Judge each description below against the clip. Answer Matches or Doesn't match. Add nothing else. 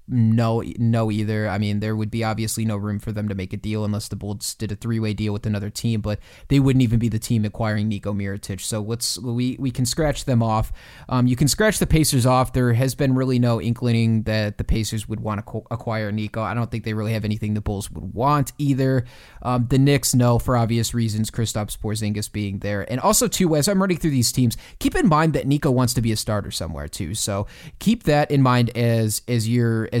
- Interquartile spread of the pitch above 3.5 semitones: Doesn't match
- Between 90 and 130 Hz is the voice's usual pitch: Matches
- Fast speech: Matches